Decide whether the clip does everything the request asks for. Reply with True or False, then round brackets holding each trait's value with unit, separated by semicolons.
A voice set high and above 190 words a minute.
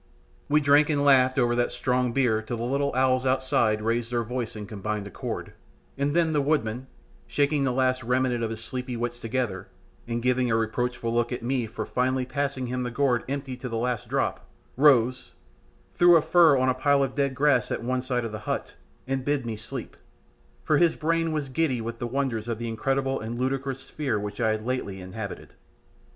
False (125 Hz; 205 wpm)